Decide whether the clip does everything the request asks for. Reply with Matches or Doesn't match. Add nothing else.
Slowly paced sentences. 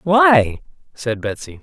Matches